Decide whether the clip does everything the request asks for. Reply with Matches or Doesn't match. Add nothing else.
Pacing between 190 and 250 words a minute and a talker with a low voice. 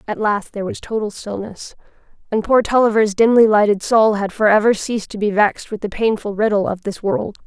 Doesn't match